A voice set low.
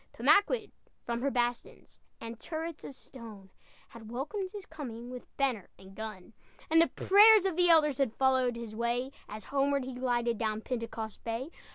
No: very high, 250 Hz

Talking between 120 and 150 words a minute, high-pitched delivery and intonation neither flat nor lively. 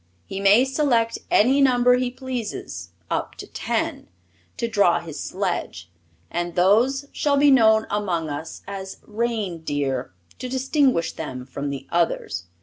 No: average, 140 wpm; high, 210 Hz; wide, 7.3 semitones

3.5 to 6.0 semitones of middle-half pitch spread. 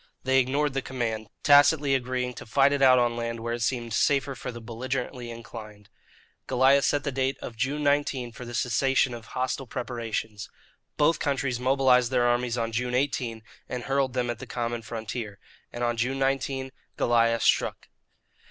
No: narrow, 2.4 semitones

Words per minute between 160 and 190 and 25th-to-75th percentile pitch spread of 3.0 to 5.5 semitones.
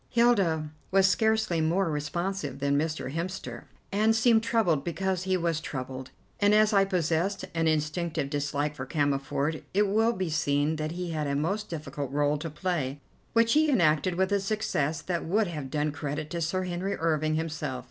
Yes: average, 180 wpm; average, 4.6 semitones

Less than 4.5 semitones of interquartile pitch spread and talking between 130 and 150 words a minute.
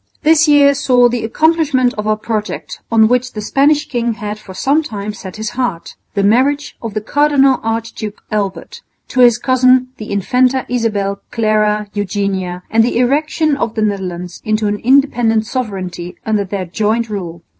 No: average, 3.8 semitones; average, 165 wpm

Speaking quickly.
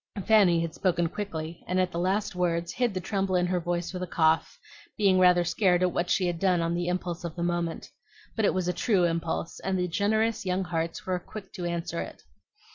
Yes: fast, 225 wpm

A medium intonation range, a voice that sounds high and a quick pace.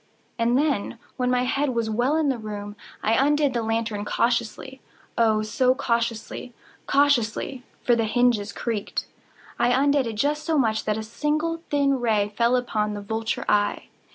No: average, 3.8 semitones; high, 235 Hz; average, 155 wpm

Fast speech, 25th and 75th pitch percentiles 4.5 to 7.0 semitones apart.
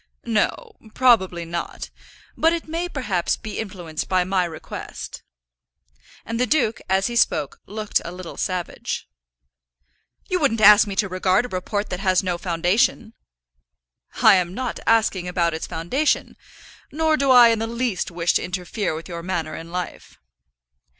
No: average, 155 wpm; average, 4.9 semitones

